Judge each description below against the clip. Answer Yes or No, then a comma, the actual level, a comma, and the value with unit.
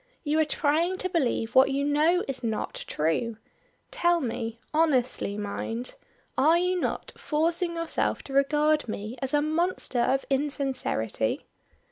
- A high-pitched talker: Yes, very high, 285 Hz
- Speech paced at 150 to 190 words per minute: No, average, 140 wpm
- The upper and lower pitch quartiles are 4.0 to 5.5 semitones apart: Yes, average, 5.2 semitones